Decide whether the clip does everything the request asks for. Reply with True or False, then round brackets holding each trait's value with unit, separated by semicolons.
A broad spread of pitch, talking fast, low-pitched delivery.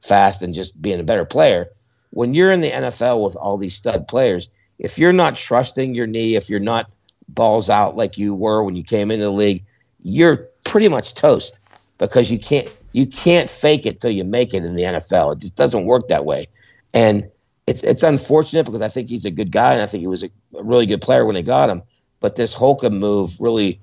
False (4.1 semitones; 225 wpm; 110 Hz)